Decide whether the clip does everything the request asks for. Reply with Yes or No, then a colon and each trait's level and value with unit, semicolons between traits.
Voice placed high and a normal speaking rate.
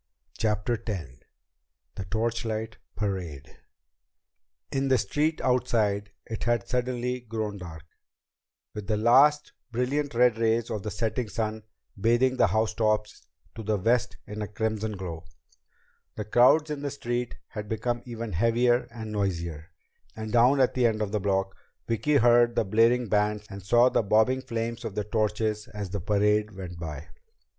No: low, 110 Hz; average, 155 wpm